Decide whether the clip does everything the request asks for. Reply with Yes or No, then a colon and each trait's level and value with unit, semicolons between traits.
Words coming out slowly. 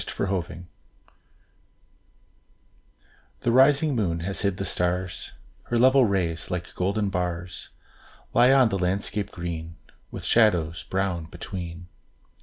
Yes: slow, 110 wpm